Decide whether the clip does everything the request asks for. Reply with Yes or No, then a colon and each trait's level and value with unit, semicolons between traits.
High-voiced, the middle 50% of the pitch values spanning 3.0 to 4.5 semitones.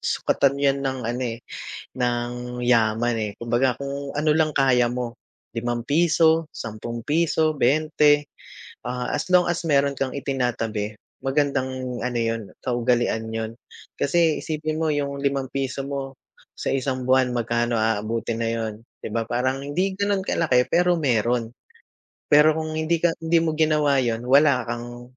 No: low, 130 Hz; average, 3.9 semitones